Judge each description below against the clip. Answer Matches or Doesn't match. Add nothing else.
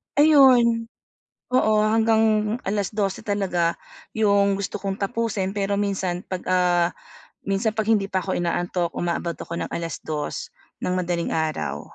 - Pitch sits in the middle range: Doesn't match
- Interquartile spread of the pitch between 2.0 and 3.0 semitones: Doesn't match